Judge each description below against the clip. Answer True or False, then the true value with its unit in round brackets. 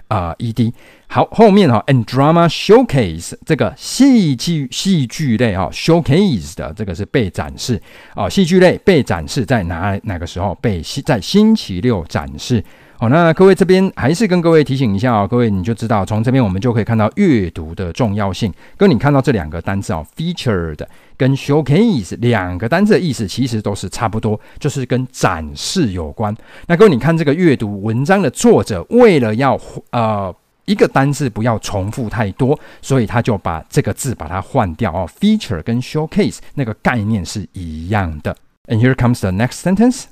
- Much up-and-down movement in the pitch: True (7.1 semitones)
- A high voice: False (120 Hz)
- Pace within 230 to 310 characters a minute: False (375 characters per minute)